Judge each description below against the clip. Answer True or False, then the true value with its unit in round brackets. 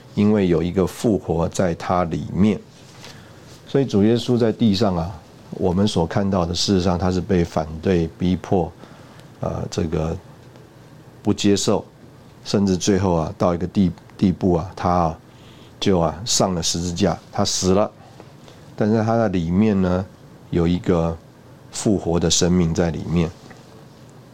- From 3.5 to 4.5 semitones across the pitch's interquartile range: False (5.2 semitones)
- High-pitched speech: False (100 Hz)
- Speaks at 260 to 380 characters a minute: False (205 characters per minute)